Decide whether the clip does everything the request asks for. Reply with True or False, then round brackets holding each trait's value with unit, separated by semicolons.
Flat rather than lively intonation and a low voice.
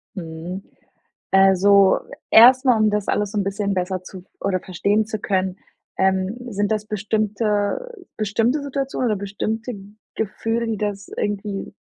False (2.3 semitones; 205 Hz)